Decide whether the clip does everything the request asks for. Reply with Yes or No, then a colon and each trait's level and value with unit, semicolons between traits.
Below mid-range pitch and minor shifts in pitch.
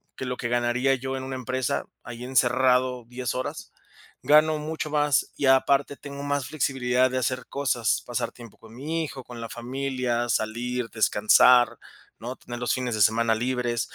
Yes: low, 125 Hz; narrow, 1.8 semitones